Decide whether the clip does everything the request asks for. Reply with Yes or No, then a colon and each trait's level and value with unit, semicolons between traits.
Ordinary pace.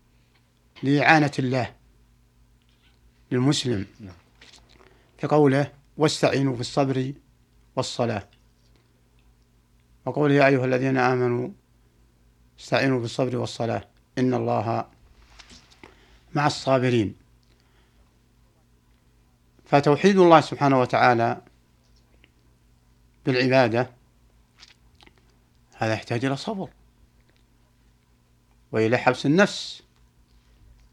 No: slow, 60 wpm